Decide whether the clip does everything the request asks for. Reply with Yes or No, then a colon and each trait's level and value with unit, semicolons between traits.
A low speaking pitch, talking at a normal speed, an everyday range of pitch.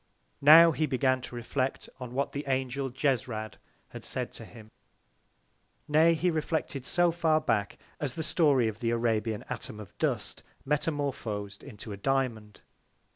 Yes: low, 130 Hz; average, 150 wpm; average, 4.8 semitones